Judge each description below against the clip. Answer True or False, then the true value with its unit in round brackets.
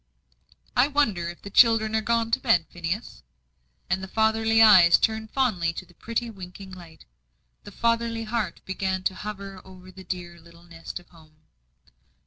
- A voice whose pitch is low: False (190 Hz)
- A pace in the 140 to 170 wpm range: True (165 wpm)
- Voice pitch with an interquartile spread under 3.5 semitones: False (4.2 semitones)